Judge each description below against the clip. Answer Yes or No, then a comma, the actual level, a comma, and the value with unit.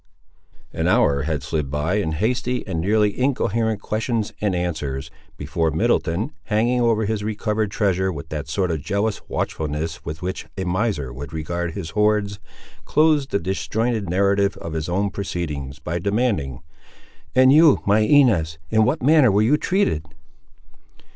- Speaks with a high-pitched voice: No, low, 100 Hz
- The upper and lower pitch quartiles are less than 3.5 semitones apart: No, wide, 5.6 semitones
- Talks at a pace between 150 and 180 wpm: Yes, average, 155 wpm